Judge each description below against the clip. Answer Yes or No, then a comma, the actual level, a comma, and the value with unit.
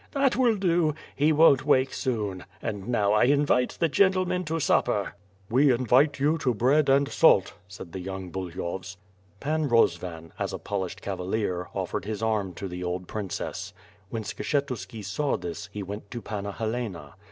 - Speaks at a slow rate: No, average, 170 wpm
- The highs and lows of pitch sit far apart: Yes, wide, 6.8 semitones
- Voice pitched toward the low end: Yes, low, 110 Hz